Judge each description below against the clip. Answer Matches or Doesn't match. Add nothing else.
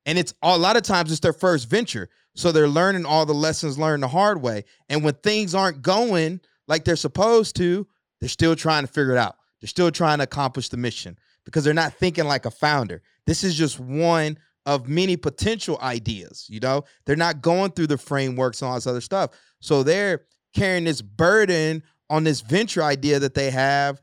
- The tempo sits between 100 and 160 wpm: Doesn't match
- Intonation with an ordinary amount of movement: Matches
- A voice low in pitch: Doesn't match